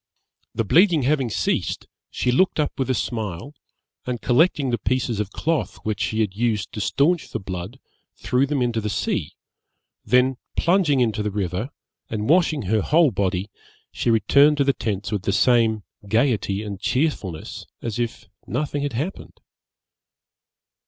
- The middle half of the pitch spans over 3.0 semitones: Yes, average, 5.1 semitones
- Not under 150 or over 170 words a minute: Yes, average, 160 wpm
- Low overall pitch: Yes, low, 120 Hz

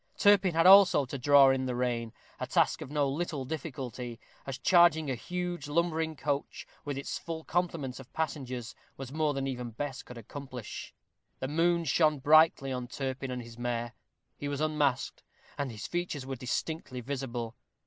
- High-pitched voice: No, medium, 140 Hz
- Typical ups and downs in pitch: Yes, average, 3.9 semitones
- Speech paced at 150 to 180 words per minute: Yes, average, 170 wpm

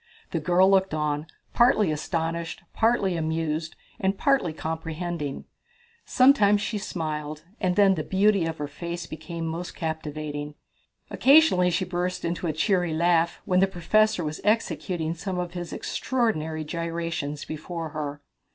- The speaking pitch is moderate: Yes, medium, 170 Hz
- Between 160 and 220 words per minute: No, average, 140 wpm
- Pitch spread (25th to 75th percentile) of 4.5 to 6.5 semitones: No, average, 3.2 semitones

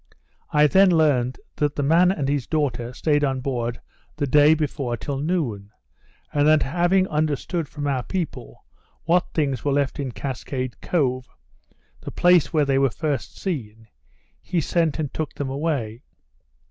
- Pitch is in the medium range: Yes, medium, 145 Hz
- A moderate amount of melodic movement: Yes, average, 3.3 semitones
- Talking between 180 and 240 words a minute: No, average, 160 wpm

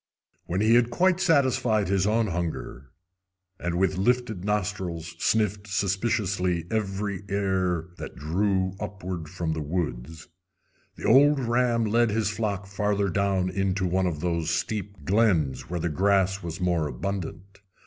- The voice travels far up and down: No, average, 3.3 semitones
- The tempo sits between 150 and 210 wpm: No, average, 140 wpm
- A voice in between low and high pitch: No, very low, 95 Hz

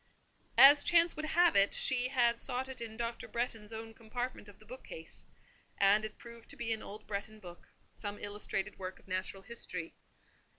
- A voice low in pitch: No, high, 225 Hz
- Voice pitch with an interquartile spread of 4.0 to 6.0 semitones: No, average, 3.5 semitones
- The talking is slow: No, average, 175 wpm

